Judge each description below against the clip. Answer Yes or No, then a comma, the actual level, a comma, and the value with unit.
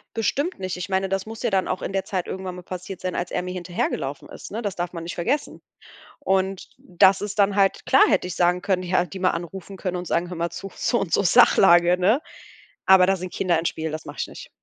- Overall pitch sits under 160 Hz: No, medium, 185 Hz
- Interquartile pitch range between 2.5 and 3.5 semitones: No, narrow, 1.7 semitones